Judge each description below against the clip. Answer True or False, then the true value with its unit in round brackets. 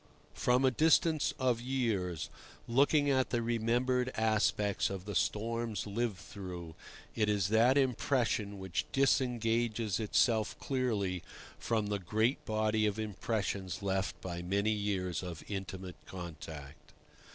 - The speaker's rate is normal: False (125 wpm)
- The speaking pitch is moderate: False (110 Hz)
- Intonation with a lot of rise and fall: False (3.8 semitones)